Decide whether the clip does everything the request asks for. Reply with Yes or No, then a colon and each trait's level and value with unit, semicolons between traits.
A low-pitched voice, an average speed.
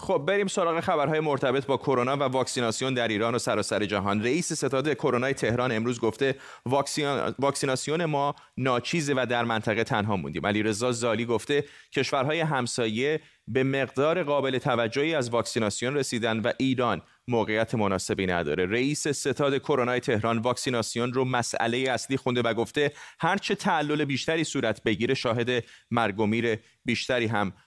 Yes: low, 125 Hz; average, 145 wpm